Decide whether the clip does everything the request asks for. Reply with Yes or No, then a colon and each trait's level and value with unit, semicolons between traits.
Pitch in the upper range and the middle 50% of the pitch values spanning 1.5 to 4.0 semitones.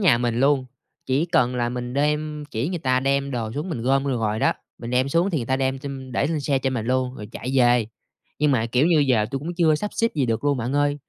No: low, 135 Hz; average, 3.2 semitones